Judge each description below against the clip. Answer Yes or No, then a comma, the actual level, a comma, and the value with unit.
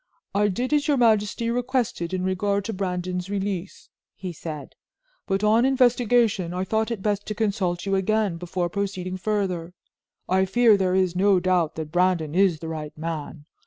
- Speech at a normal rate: Yes, average, 170 wpm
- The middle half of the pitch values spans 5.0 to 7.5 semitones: No, average, 3.1 semitones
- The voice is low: No, high, 190 Hz